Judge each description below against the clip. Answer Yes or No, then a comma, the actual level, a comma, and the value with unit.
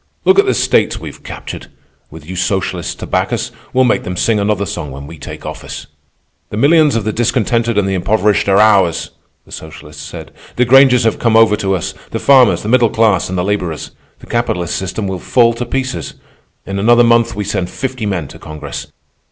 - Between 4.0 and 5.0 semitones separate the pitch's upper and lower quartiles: Yes, average, 4.6 semitones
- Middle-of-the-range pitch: No, low, 105 Hz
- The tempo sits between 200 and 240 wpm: Yes, fast, 205 wpm